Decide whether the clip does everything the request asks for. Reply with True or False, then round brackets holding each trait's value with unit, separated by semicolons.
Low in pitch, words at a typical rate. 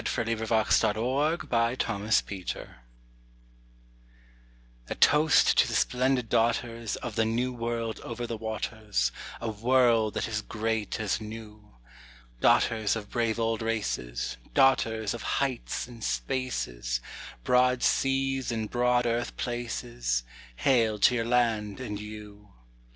False (115 Hz; 125 wpm)